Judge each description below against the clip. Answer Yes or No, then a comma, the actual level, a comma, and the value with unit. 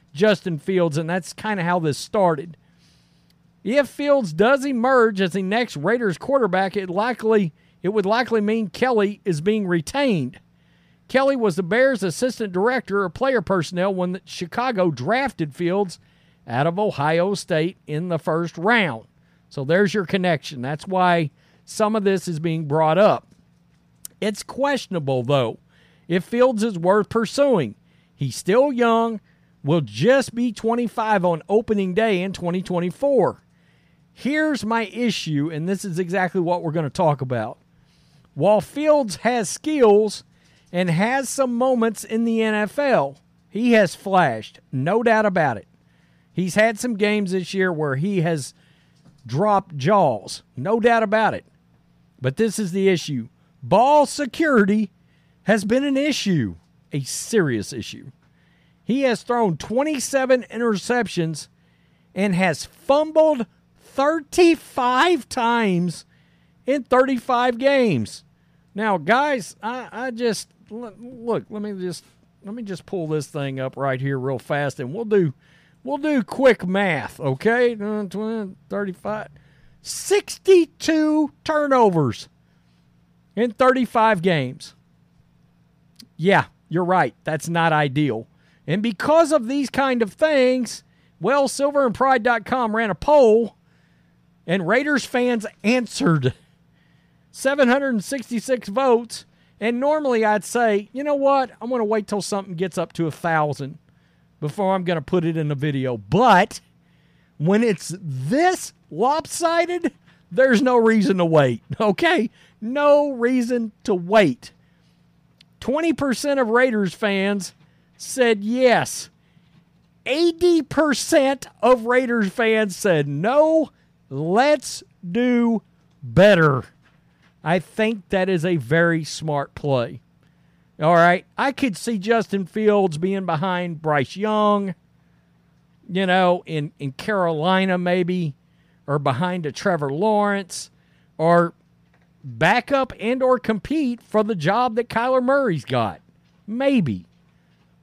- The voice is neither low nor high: No, high, 200 Hz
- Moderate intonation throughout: No, wide, 6.3 semitones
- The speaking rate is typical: No, slow, 125 wpm